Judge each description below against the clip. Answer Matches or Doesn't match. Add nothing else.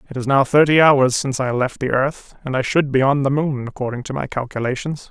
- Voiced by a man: Matches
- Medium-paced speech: Doesn't match